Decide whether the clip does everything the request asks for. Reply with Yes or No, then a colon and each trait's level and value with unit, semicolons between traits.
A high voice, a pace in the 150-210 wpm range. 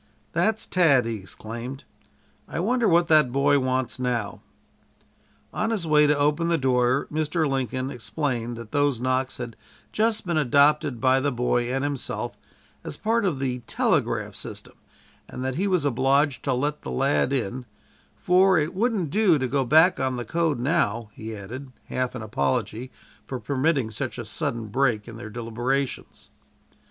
No: low, 135 Hz; average, 165 wpm